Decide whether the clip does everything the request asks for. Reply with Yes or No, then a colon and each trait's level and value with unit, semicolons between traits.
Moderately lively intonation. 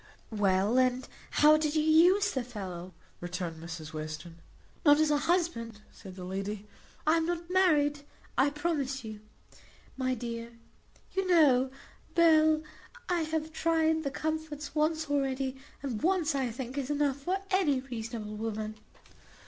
No: wide, 6.0 semitones